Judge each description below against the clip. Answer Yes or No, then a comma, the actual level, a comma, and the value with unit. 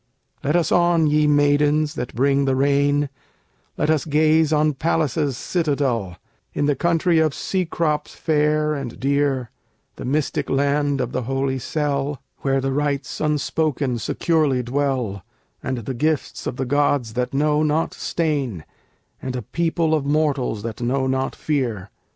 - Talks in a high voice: No, medium, 145 Hz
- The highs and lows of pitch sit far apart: No, narrow, 2.6 semitones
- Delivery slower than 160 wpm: Yes, average, 150 wpm